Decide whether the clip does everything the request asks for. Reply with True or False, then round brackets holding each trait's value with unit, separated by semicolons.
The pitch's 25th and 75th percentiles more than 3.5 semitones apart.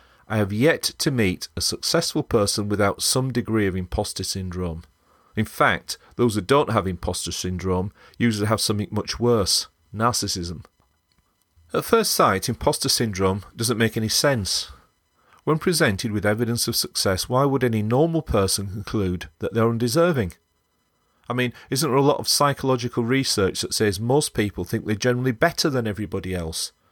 True (4.7 semitones)